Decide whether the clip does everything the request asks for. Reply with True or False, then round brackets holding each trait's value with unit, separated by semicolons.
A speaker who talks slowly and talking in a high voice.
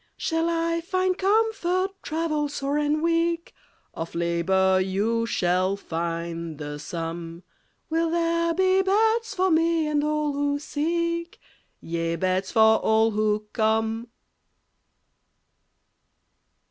True (110 wpm; 290 Hz)